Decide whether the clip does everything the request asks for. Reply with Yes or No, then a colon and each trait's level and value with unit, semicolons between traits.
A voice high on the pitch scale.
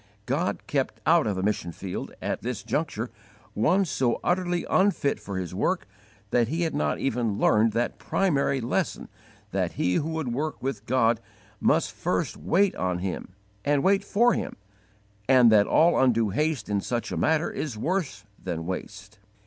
No: low, 125 Hz